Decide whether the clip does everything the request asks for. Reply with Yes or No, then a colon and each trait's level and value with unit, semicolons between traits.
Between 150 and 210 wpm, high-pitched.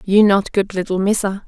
Yes: fast, 205 wpm; high, 195 Hz